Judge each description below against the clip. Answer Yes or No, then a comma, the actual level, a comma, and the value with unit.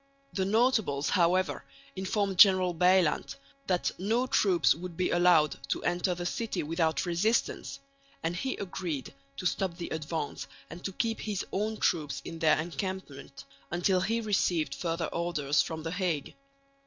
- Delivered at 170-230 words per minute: No, average, 150 wpm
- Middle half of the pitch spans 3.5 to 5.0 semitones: No, average, 3.0 semitones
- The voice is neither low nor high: Yes, medium, 175 Hz